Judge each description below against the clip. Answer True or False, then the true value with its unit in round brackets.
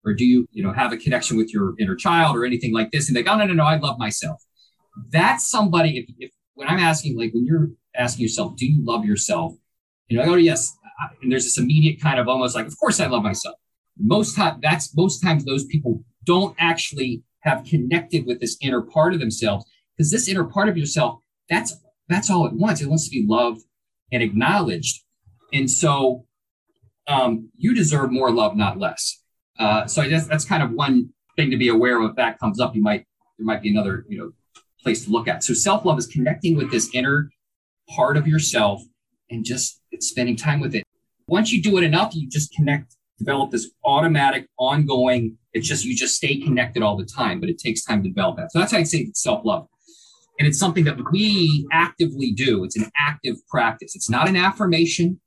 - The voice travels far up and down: True (5.8 semitones)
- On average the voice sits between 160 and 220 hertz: False (145 Hz)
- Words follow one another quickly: True (215 wpm)